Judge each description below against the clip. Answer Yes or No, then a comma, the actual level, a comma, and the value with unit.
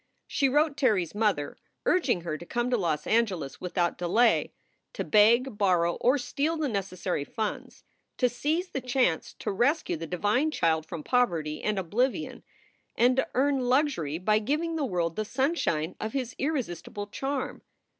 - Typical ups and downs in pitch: No, wide, 7.4 semitones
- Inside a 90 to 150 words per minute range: No, average, 165 wpm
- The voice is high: Yes, high, 220 Hz